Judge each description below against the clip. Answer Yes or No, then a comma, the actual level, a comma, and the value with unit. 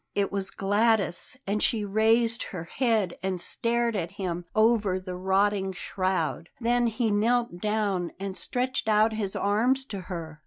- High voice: Yes, high, 205 Hz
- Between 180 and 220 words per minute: No, average, 155 wpm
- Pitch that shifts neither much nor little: Yes, average, 3.2 semitones